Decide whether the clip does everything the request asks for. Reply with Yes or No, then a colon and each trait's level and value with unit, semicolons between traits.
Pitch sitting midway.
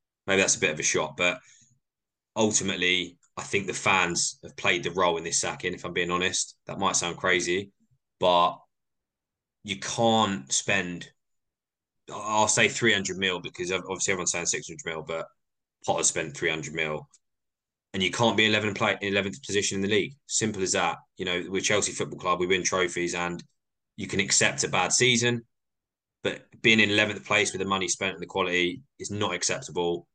No: very low, 95 Hz